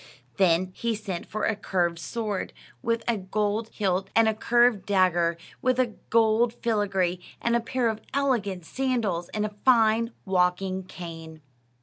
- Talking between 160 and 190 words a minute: No, average, 145 wpm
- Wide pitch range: No, average, 3.9 semitones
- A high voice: Yes, high, 210 Hz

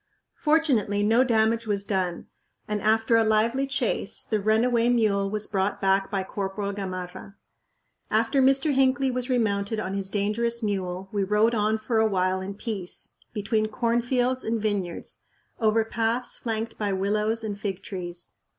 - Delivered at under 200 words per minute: Yes, average, 155 wpm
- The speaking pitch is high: Yes, high, 215 Hz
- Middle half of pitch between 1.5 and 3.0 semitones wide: Yes, average, 2.7 semitones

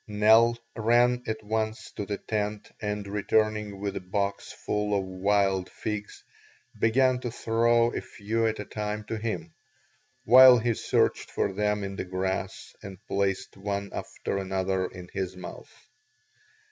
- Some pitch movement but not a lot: No, narrow, 2.3 semitones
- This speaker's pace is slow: No, average, 150 wpm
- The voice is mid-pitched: No, low, 105 Hz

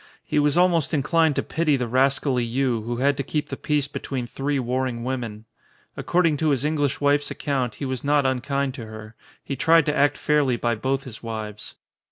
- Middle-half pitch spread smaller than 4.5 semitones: Yes, average, 3.3 semitones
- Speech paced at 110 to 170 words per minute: No, fast, 205 wpm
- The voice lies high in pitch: No, low, 135 Hz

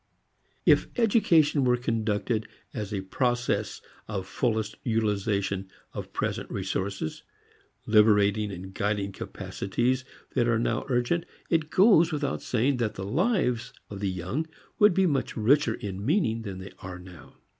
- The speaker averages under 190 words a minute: Yes, average, 140 wpm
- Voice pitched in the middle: No, low, 110 Hz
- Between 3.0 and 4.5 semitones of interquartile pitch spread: No, average, 5.3 semitones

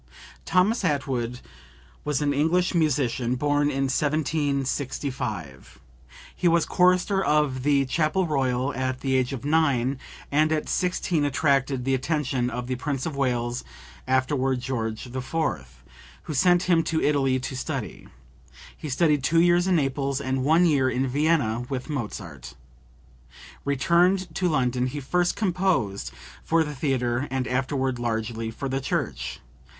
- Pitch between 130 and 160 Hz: Yes, medium, 140 Hz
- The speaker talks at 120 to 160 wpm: Yes, average, 140 wpm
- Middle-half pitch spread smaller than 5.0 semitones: Yes, average, 3.6 semitones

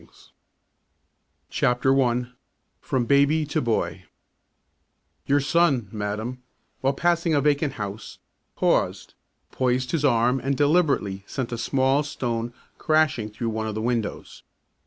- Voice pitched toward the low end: Yes, low, 130 Hz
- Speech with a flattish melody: No, average, 3.8 semitones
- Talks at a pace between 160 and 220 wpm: No, slow, 135 wpm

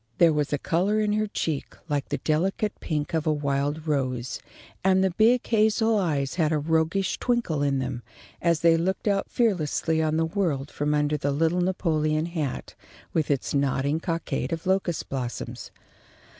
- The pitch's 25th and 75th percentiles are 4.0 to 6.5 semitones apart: Yes, average, 4.3 semitones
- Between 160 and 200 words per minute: Yes, average, 170 wpm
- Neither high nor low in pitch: Yes, medium, 160 Hz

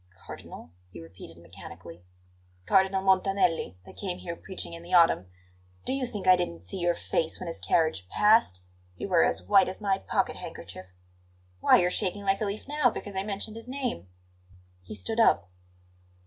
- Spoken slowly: No, average, 175 wpm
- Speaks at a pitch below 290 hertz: Yes, medium, 185 Hz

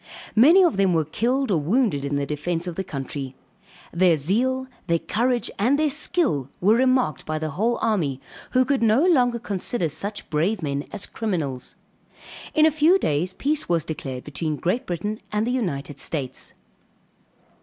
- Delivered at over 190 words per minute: No, average, 170 wpm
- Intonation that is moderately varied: No, wide, 8.5 semitones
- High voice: Yes, high, 195 Hz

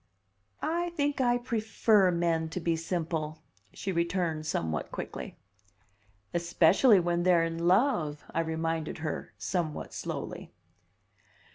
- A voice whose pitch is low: No, medium, 170 Hz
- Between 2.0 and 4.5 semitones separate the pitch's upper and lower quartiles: Yes, average, 3.7 semitones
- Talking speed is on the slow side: Yes, slow, 115 wpm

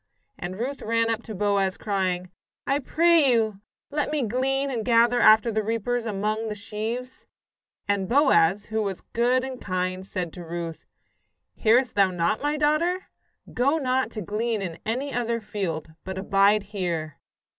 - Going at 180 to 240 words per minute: No, average, 160 wpm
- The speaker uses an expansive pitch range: No, average, 4.6 semitones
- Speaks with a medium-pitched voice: No, high, 220 Hz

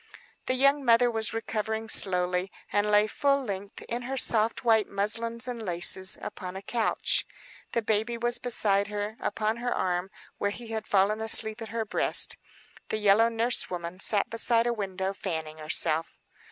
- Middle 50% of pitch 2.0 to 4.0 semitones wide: Yes, average, 2.9 semitones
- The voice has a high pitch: Yes, high, 215 Hz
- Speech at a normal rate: Yes, average, 165 wpm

